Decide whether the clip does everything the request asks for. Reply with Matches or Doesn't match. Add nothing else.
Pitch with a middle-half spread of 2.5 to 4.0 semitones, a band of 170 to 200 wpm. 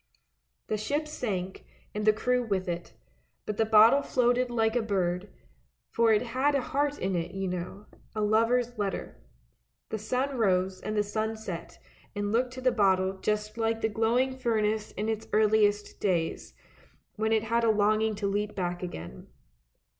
Matches